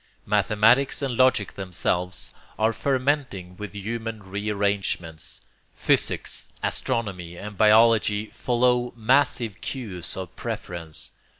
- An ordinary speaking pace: No, slow, 95 wpm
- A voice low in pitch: Yes, low, 105 Hz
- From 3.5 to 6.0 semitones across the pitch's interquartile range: Yes, average, 4.0 semitones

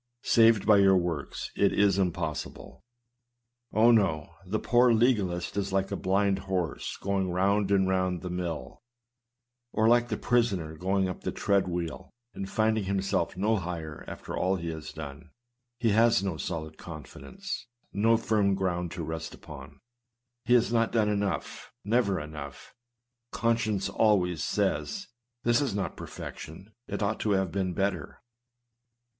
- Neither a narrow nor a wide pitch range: Yes, average, 3.7 semitones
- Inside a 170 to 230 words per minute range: No, average, 150 wpm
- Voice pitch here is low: Yes, very low, 95 Hz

